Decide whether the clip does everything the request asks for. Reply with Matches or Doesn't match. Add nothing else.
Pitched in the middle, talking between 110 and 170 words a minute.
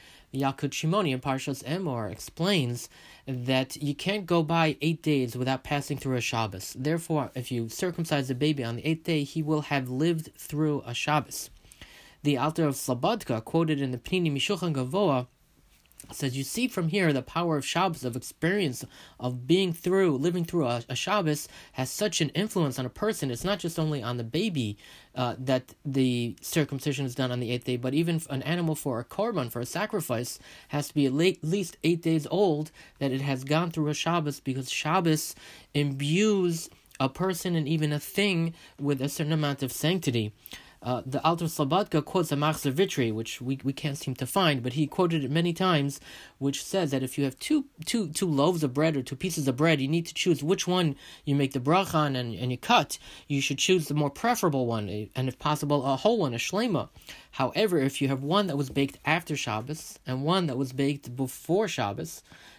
Doesn't match